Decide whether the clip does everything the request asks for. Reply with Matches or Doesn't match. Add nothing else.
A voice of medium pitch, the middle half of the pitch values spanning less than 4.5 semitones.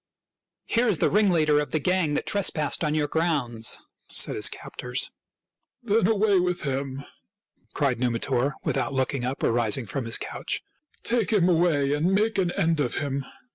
Doesn't match